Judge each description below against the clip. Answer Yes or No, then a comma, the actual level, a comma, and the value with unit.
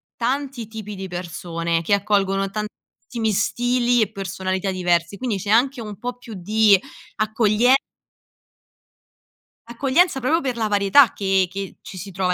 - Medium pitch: No, high, 210 Hz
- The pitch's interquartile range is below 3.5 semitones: No, average, 4.0 semitones